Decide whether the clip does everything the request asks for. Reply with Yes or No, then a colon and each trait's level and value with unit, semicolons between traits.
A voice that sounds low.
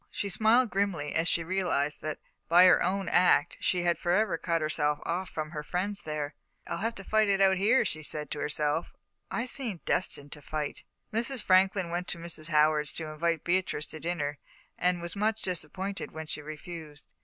No: medium, 170 Hz